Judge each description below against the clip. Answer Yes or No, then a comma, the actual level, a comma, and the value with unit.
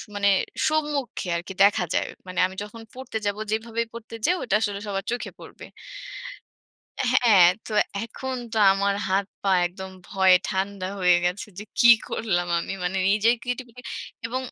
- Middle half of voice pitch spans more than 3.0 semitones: Yes, average, 3.6 semitones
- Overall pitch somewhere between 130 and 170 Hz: No, high, 205 Hz